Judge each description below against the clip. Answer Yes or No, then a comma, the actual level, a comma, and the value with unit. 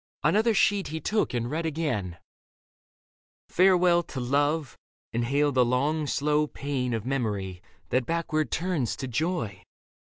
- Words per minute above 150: No, slow, 135 wpm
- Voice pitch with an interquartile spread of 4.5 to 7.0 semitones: Yes, average, 5.1 semitones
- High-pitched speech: No, medium, 145 Hz